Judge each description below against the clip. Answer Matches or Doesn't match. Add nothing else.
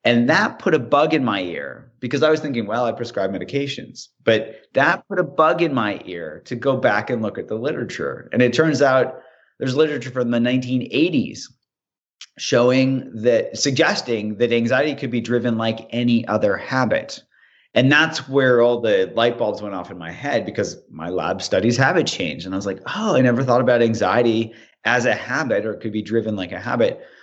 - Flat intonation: Doesn't match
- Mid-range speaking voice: Doesn't match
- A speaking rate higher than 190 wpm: Matches